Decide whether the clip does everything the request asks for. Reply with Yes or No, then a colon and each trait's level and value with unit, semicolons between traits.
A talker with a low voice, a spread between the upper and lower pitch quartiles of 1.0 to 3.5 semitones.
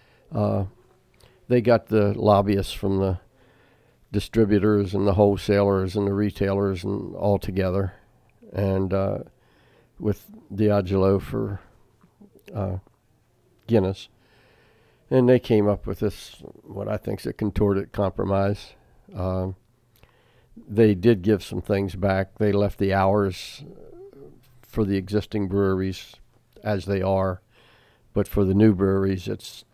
Yes: low, 105 Hz; average, 2.8 semitones